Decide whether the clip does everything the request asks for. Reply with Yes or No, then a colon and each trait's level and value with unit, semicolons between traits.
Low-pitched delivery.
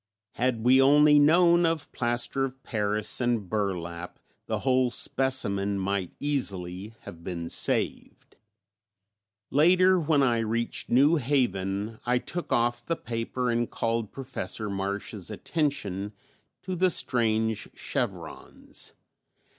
Yes: low, 120 Hz